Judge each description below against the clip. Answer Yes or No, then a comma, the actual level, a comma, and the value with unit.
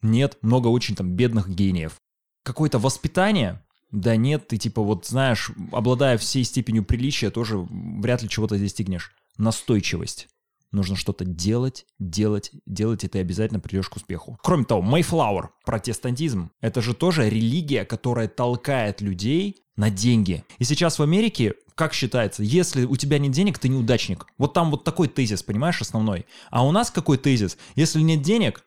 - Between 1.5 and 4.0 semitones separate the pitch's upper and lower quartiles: No, average, 4.9 semitones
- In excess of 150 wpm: Yes, fast, 160 wpm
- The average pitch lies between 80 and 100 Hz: No, low, 120 Hz